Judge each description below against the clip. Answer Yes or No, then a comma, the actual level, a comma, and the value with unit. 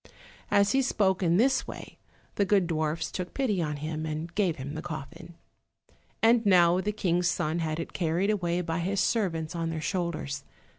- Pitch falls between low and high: Yes, medium, 175 Hz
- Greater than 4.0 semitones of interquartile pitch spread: No, average, 3.6 semitones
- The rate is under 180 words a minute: No, average, 185 wpm